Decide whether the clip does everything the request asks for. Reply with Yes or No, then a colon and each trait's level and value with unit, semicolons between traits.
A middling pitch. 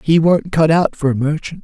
Yes: medium, 155 Hz